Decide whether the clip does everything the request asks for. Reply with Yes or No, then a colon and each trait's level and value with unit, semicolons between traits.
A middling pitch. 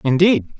Yes: medium, 155 Hz